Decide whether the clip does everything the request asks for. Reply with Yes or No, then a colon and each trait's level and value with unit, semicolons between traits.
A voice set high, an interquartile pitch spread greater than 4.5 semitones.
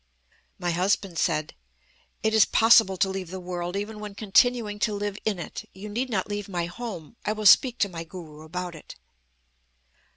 No: high, 195 Hz; average, 3.3 semitones